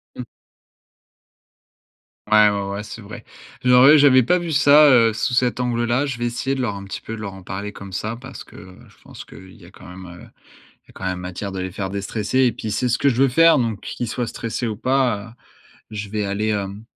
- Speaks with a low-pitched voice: Yes, low, 110 Hz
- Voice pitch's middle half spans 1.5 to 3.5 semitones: No, average, 4.0 semitones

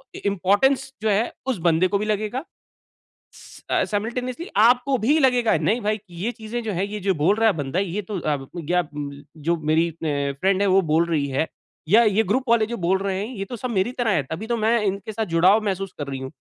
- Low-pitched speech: No, high, 200 Hz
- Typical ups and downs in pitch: Yes, average, 4.4 semitones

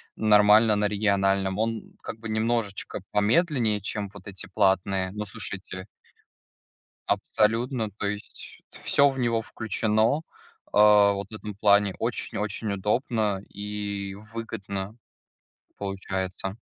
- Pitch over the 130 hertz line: No, low, 105 Hz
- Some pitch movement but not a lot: No, narrow, 1.9 semitones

